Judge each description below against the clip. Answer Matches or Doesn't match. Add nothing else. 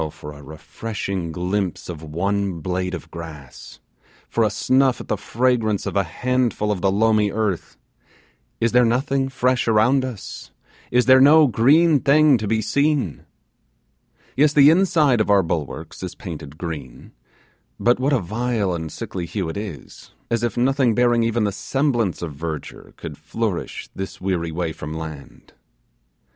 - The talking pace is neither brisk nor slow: Matches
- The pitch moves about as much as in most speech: Doesn't match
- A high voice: Doesn't match